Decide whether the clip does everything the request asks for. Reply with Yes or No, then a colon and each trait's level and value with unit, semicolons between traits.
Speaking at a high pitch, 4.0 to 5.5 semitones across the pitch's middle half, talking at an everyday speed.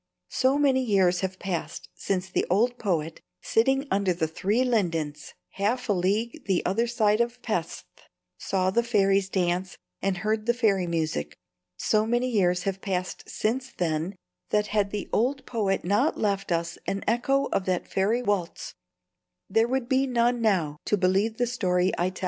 Yes: high, 200 Hz; average, 4.4 semitones; average, 170 wpm